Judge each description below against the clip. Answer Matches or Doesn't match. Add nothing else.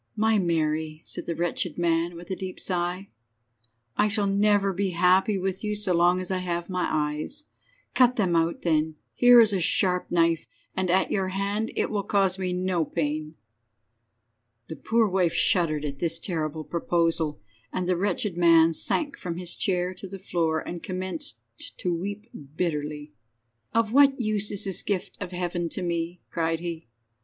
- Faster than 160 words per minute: Matches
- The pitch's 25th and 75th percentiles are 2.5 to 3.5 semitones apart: Matches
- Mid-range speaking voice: Matches